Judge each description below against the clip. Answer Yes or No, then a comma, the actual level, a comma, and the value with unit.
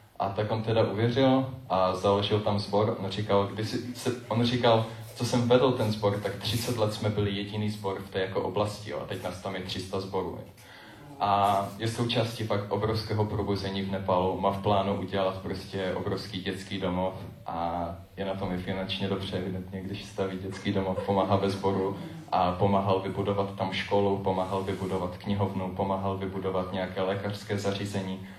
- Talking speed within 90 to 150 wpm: No, average, 165 wpm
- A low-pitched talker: Yes, low, 100 Hz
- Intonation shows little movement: Yes, narrow, 1.7 semitones